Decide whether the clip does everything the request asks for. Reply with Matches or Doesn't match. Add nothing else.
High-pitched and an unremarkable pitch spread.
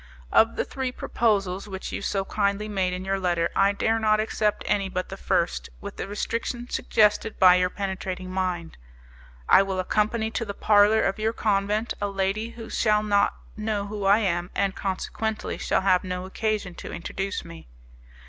Doesn't match